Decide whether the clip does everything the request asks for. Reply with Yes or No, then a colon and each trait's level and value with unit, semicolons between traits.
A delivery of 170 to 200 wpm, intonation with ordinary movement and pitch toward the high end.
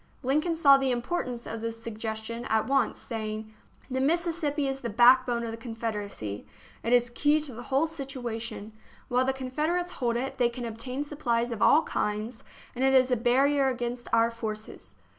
Yes: average, 195 wpm; average, 3.0 semitones; high, 245 Hz